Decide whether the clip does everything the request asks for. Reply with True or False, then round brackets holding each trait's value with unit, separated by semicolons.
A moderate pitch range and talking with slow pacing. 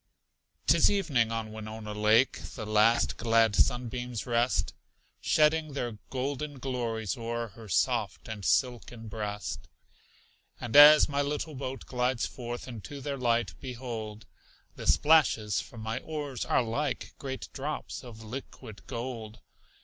True (3.4 semitones; 130 wpm)